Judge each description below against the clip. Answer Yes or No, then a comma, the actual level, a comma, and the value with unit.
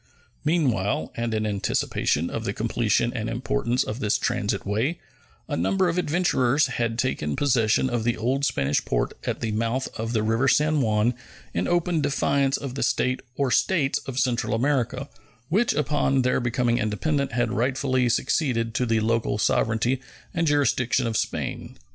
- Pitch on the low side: Yes, low, 125 Hz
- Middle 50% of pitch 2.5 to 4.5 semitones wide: Yes, average, 3.5 semitones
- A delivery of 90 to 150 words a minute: No, average, 165 wpm